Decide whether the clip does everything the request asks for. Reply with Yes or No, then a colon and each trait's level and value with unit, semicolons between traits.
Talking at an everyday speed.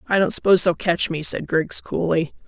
No: fast, 220 wpm